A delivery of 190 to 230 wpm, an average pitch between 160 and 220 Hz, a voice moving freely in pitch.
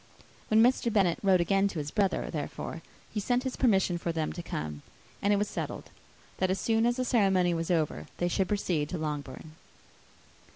No: average, 195 wpm; high, 190 Hz; average, 4.0 semitones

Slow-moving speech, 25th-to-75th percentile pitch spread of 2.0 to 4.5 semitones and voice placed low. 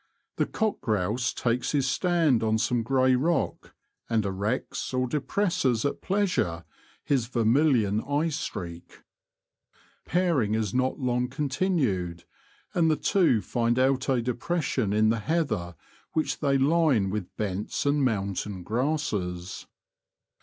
No: slow, 130 wpm; wide, 5.6 semitones; low, 125 Hz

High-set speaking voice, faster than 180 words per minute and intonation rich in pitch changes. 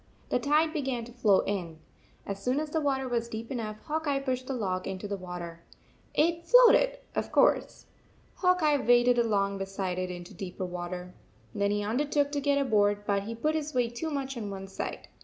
Yes: high, 235 Hz; average, 200 wpm; wide, 6.4 semitones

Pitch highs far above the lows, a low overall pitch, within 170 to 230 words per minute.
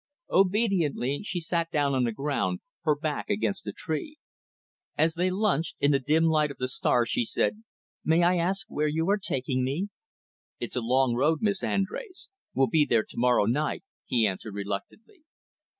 No: wide, 6.1 semitones; medium, 155 Hz; average, 180 wpm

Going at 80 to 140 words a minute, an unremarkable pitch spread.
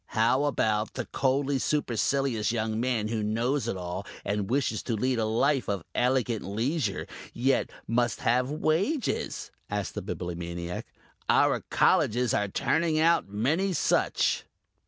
Yes: slow, 135 wpm; average, 4.6 semitones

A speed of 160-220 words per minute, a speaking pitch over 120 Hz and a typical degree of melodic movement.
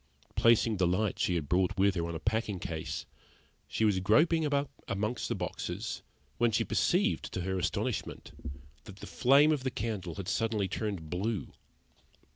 No: average, 170 wpm; low, 105 Hz; average, 4.2 semitones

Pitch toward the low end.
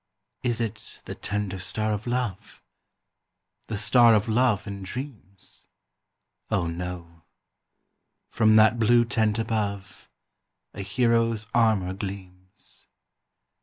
Yes: low, 105 Hz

